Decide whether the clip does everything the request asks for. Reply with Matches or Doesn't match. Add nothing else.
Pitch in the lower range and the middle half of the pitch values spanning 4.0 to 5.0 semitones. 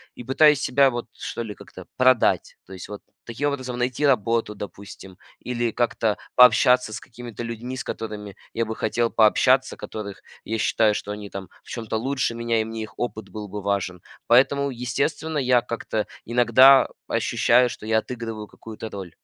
Doesn't match